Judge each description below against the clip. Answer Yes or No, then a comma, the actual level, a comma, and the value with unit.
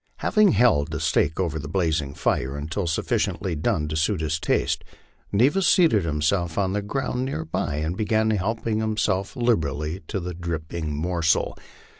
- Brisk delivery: No, average, 160 wpm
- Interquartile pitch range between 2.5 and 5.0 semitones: No, wide, 5.6 semitones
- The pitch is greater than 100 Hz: No, very low, 85 Hz